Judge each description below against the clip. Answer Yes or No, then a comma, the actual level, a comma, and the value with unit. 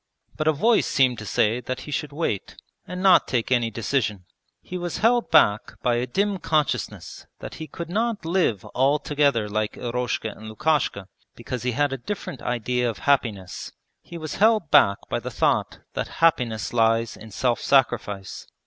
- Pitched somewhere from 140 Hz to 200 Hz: No, low, 130 Hz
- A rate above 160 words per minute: Yes, average, 175 wpm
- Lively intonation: Yes, wide, 5.9 semitones